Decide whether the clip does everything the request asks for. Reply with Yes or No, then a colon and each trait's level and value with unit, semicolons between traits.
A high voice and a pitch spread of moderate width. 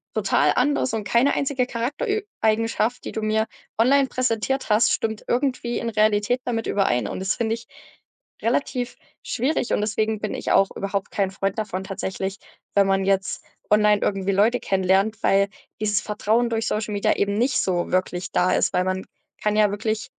Yes: high, 215 Hz; average, 3.1 semitones